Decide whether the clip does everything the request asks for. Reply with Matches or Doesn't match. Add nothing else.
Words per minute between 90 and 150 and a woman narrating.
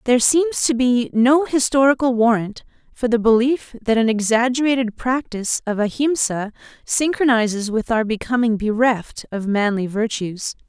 Matches